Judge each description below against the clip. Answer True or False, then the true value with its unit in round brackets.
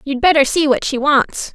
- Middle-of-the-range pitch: False (280 Hz)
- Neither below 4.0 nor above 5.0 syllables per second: True (4.8 syllables/s)